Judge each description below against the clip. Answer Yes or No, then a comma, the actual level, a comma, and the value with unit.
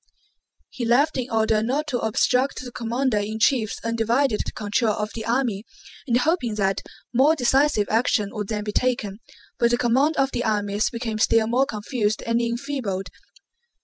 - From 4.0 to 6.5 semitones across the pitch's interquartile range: No, average, 3.1 semitones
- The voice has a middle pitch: No, high, 230 Hz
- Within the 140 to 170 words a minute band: Yes, average, 165 wpm